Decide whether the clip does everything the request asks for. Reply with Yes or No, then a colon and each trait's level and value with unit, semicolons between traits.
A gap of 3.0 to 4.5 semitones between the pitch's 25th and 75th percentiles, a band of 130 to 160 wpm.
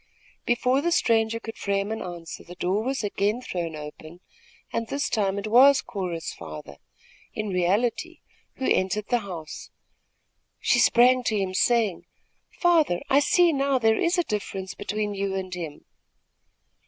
No: average, 5.2 semitones; average, 155 wpm